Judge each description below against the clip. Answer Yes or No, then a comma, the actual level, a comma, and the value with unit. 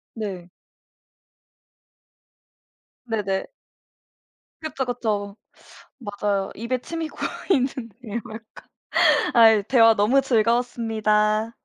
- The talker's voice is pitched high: Yes, high, 225 Hz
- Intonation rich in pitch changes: No, average, 2.9 semitones